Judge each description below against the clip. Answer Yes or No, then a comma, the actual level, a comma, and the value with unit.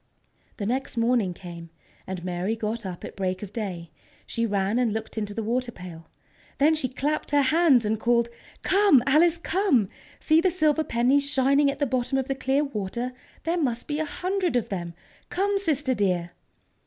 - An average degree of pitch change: No, wide, 6.2 semitones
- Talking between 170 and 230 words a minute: Yes, average, 185 wpm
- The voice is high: Yes, high, 245 Hz